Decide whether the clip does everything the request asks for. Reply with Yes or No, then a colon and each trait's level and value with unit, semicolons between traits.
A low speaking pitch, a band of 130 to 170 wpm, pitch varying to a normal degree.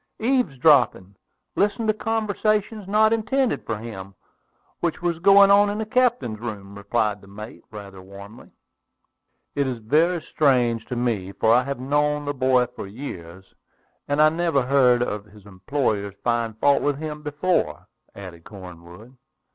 No: low, 130 Hz; average, 155 wpm; wide, 8.5 semitones